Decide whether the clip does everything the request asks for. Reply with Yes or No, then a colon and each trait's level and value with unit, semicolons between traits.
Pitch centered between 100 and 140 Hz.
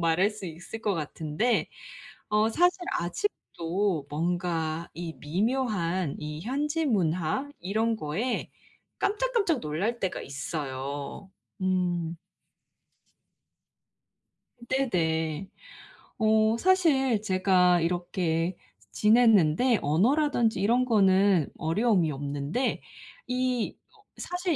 No: high, 190 Hz